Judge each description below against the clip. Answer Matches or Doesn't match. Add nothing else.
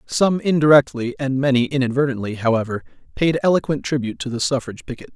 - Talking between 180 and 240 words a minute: Doesn't match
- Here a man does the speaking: Matches